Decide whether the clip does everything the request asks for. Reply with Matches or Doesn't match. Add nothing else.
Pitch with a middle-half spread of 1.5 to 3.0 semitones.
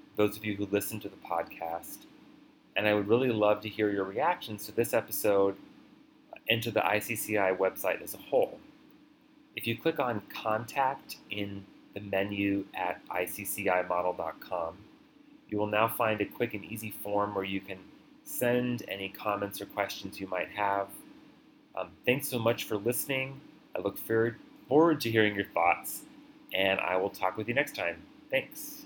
Doesn't match